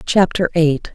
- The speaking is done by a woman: Yes, female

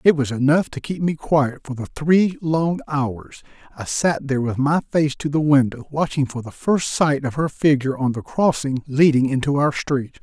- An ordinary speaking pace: No, fast, 210 wpm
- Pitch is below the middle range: No, medium, 145 Hz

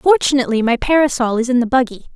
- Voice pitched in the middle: No, very high, 255 Hz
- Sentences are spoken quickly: No, average, 195 wpm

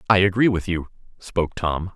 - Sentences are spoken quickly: No, average, 185 wpm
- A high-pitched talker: No, very low, 95 Hz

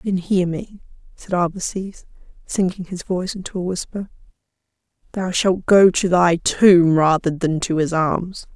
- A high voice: No, medium, 180 Hz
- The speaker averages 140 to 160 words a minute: Yes, average, 155 wpm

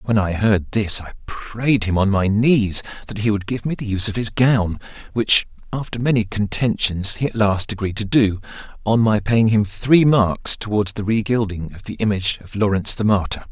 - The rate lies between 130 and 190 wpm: No, fast, 205 wpm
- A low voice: Yes, low, 105 Hz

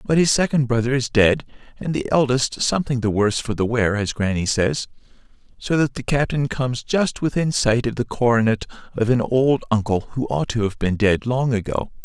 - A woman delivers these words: No, male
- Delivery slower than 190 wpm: No, fast, 205 wpm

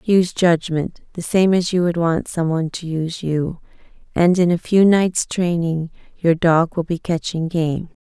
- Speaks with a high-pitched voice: No, medium, 170 Hz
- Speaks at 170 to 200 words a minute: Yes, average, 185 wpm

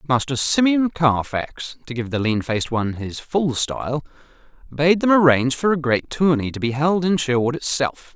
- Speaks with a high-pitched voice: No, medium, 145 Hz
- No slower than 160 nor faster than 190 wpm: Yes, average, 185 wpm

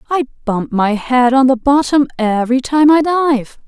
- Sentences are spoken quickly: No, average, 180 wpm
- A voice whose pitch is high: Yes, very high, 260 Hz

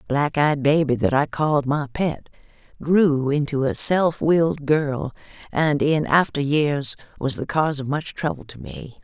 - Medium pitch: Yes, medium, 145 Hz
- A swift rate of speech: No, average, 180 wpm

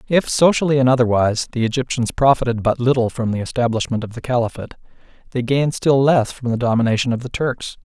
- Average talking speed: Yes, average, 190 wpm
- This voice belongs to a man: Yes, male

